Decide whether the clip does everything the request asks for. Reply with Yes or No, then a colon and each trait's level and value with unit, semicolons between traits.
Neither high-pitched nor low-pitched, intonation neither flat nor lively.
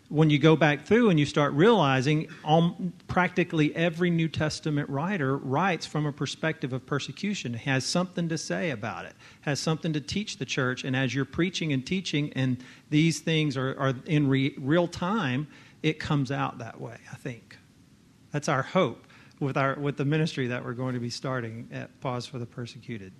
Yes: medium, 145 Hz; average, 3.6 semitones